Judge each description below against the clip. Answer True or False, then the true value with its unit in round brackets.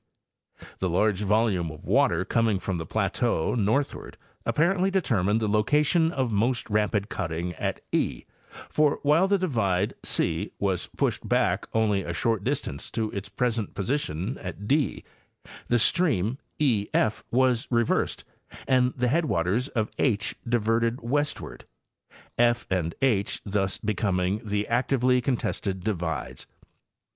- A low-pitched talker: True (110 Hz)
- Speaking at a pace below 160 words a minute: True (135 wpm)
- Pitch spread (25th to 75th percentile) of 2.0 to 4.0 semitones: False (4.7 semitones)